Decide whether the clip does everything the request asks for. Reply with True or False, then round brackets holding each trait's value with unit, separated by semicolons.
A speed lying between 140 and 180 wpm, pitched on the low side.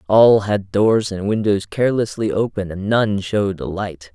True (175 wpm; 100 Hz)